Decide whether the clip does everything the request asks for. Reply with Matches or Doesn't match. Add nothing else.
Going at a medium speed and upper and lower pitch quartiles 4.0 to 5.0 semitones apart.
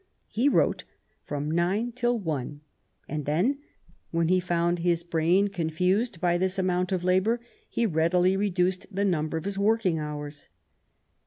Doesn't match